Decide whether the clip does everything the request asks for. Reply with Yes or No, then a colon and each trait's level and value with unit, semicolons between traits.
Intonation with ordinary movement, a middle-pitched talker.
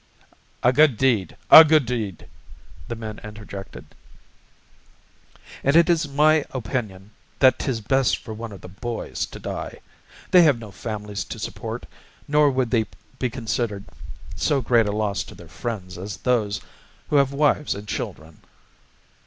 No: average, 4.7 semitones; low, 115 Hz